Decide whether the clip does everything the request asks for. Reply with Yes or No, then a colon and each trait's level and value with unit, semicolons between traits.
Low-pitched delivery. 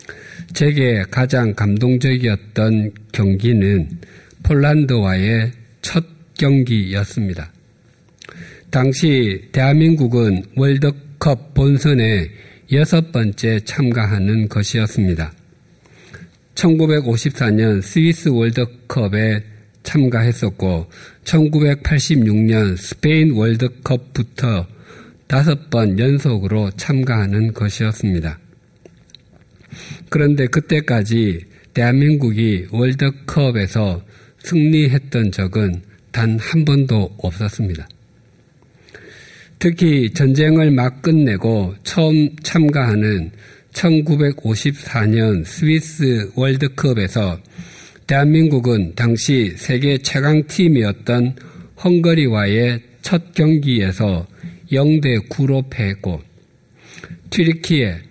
Yes: low, 120 Hz